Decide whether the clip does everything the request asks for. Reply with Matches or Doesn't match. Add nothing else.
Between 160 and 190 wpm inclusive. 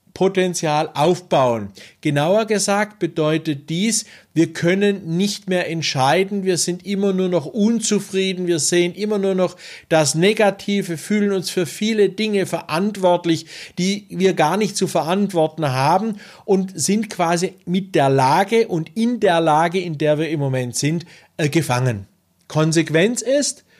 Doesn't match